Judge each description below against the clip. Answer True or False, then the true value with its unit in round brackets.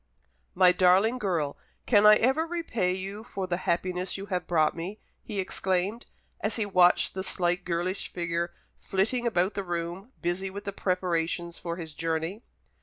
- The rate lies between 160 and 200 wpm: True (165 wpm)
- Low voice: False (185 Hz)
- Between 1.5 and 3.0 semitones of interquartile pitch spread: True (2.7 semitones)